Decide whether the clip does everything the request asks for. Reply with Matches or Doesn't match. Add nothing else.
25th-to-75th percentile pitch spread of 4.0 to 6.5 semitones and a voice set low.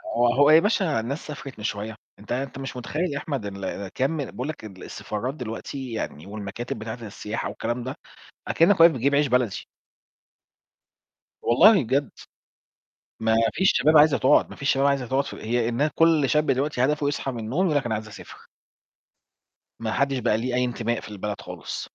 Matches